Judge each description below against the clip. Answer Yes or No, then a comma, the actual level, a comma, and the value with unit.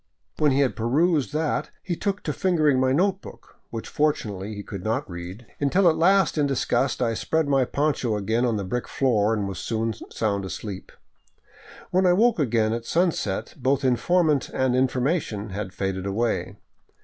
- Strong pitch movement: Yes, wide, 6.1 semitones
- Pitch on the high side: No, low, 125 Hz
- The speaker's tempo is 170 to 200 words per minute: Yes, average, 175 wpm